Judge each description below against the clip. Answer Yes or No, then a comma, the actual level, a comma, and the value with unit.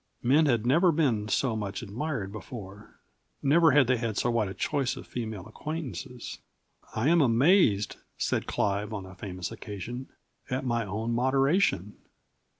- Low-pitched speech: Yes, low, 120 Hz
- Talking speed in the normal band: Yes, average, 150 wpm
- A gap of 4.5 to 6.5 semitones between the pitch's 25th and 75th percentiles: Yes, average, 4.8 semitones